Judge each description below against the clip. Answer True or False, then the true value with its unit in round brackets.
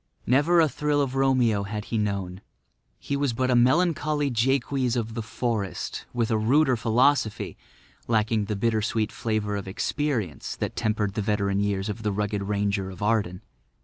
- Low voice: True (110 Hz)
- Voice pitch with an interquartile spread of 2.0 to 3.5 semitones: False (4.1 semitones)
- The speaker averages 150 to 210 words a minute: True (170 wpm)